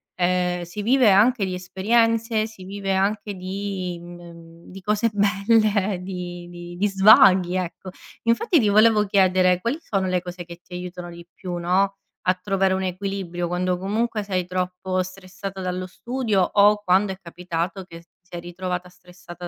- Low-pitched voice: No, medium, 185 Hz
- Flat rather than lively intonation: Yes, narrow, 2.3 semitones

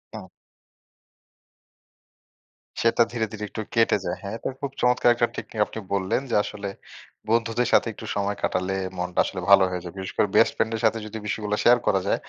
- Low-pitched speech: Yes, low, 110 Hz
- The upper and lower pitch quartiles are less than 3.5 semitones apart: Yes, average, 2.9 semitones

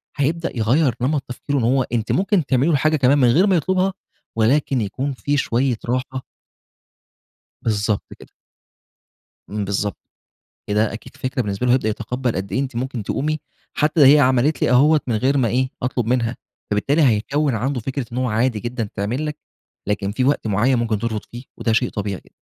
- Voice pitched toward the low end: Yes, low, 125 Hz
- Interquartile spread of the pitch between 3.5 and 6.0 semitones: Yes, average, 4.1 semitones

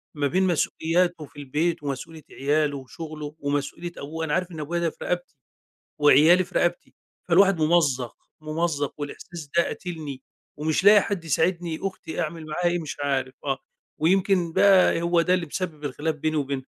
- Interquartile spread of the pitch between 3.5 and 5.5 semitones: No, average, 3.0 semitones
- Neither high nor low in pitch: Yes, medium, 160 Hz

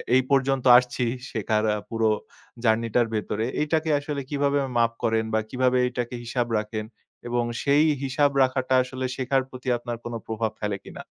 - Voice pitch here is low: Yes, low, 125 Hz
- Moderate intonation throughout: Yes, average, 3.1 semitones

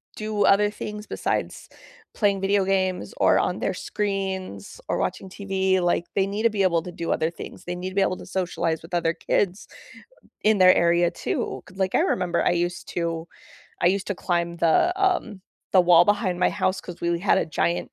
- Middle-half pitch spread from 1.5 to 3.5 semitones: Yes, narrow, 2.4 semitones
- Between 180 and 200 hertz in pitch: Yes, medium, 185 Hz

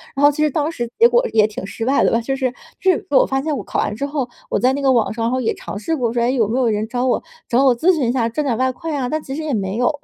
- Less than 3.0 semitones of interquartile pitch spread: No, average, 3.7 semitones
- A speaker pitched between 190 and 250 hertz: No, very high, 260 Hz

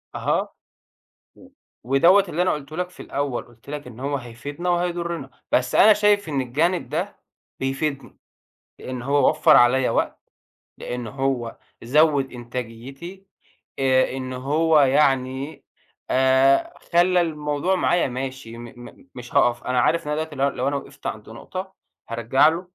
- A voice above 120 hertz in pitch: Yes, medium, 140 Hz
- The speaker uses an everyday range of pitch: Yes, average, 4.2 semitones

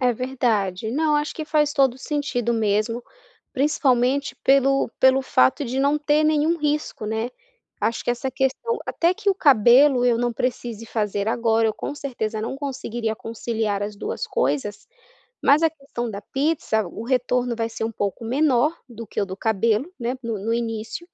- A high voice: Yes, high, 245 Hz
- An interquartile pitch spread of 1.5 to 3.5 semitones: No, average, 4.1 semitones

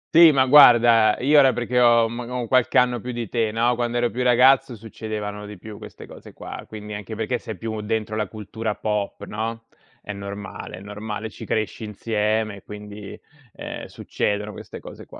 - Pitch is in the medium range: No, low, 110 Hz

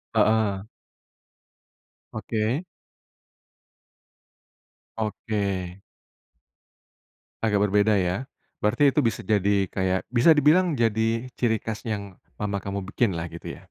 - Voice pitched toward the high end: No, low, 105 Hz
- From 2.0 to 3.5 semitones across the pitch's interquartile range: Yes, narrow, 2.6 semitones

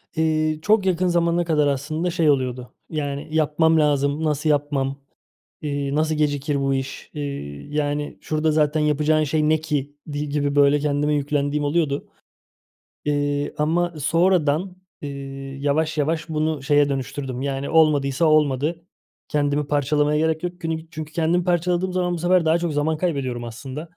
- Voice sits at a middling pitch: Yes, medium, 150 Hz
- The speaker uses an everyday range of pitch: No, narrow, 2.0 semitones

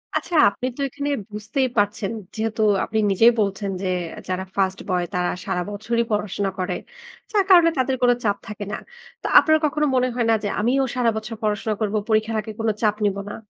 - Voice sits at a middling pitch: No, high, 215 Hz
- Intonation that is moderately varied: Yes, average, 3.4 semitones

